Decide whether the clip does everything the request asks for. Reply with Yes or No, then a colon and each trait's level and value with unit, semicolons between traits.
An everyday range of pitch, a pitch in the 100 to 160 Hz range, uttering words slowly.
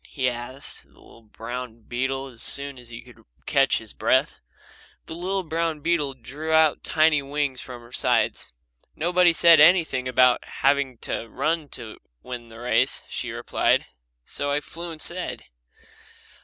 No: average, 4.4 semitones; medium, 140 Hz; average, 155 wpm